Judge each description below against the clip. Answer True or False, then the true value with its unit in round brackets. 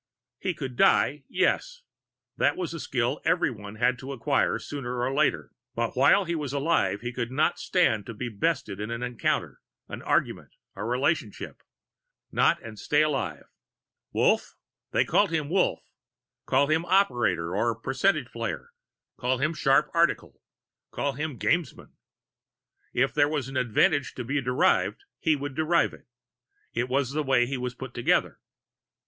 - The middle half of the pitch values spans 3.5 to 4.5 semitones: True (4.1 semitones)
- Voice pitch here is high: False (135 Hz)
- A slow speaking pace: False (155 wpm)